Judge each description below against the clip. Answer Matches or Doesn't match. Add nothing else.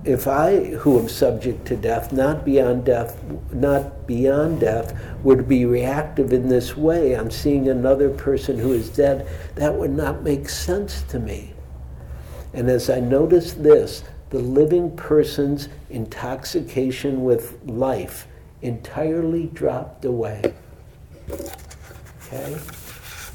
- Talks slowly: Matches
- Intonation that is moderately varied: Matches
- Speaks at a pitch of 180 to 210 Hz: Doesn't match